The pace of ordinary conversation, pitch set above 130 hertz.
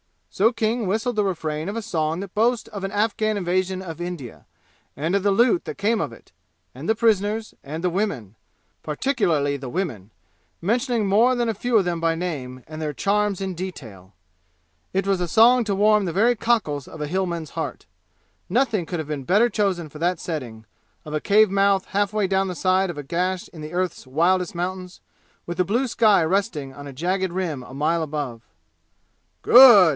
Yes: average, 195 wpm; medium, 185 Hz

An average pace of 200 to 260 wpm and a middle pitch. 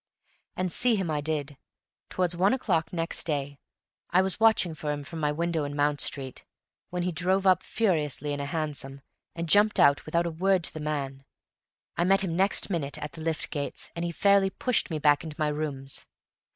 Yes: fast, 205 wpm; medium, 160 Hz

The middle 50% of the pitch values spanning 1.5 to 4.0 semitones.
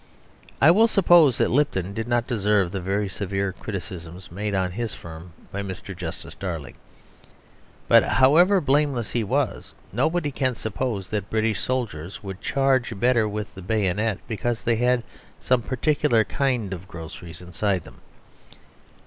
No: average, 5.1 semitones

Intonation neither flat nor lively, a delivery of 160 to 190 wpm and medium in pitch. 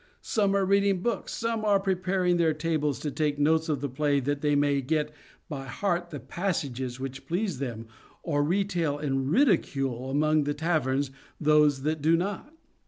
Yes: average, 4.2 semitones; average, 170 wpm; medium, 150 Hz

